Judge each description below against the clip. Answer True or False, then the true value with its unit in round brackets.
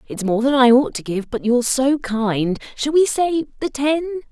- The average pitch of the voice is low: False (260 Hz)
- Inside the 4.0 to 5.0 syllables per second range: True (4.7 syllables/s)